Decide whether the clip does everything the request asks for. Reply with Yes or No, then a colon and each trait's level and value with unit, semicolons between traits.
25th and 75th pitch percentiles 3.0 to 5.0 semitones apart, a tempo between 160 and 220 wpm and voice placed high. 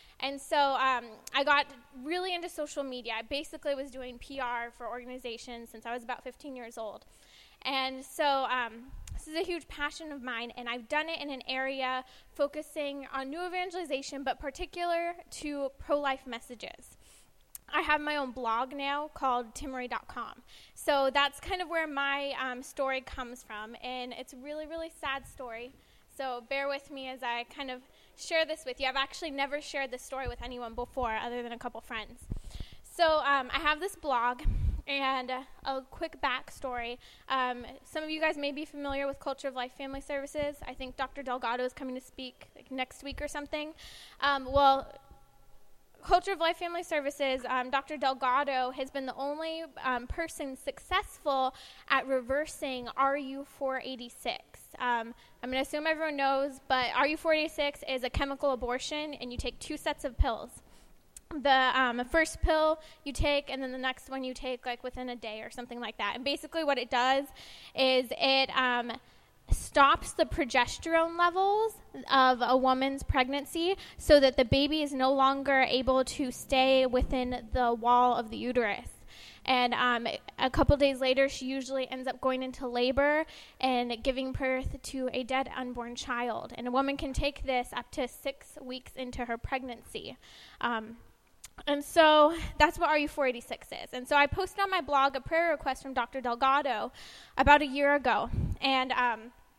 No: narrow, 2.5 semitones; average, 180 wpm; very high, 270 Hz